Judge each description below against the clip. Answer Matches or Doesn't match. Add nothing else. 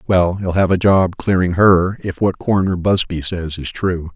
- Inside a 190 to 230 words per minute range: Matches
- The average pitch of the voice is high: Doesn't match